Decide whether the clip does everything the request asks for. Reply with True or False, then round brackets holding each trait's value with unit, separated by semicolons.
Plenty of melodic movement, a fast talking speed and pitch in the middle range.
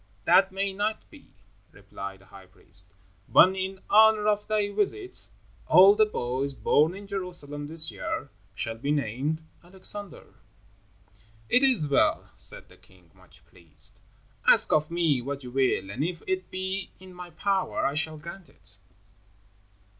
False (6.5 semitones; 155 wpm; 165 Hz)